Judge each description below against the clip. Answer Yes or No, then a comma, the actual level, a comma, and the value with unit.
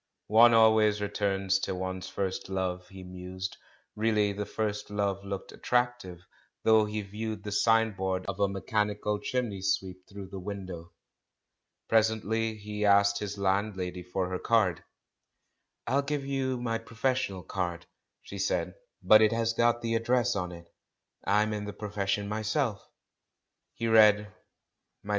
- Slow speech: No, average, 150 wpm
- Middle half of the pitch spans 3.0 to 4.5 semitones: No, narrow, 2.6 semitones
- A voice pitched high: No, low, 105 Hz